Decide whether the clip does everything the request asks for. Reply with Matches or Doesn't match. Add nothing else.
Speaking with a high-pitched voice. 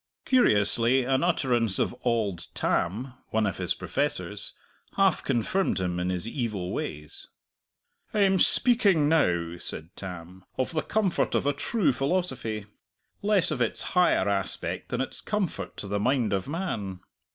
Doesn't match